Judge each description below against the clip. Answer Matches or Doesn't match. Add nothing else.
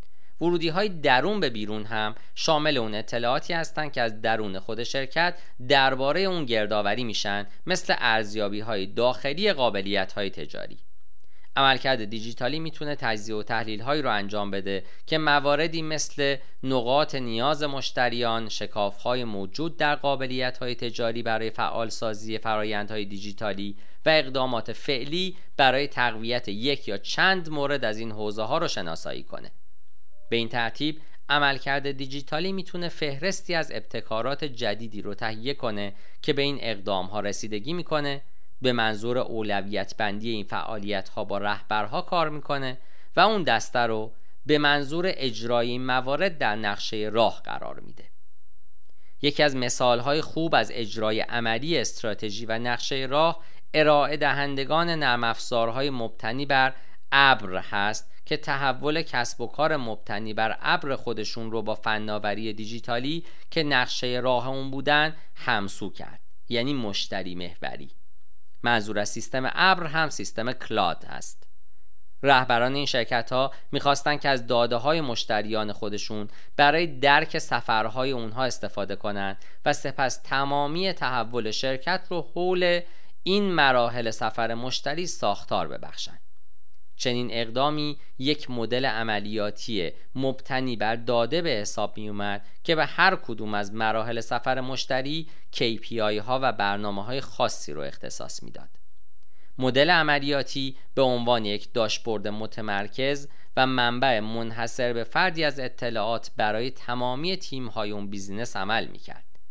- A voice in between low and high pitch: Doesn't match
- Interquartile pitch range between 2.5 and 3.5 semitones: Doesn't match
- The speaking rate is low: Doesn't match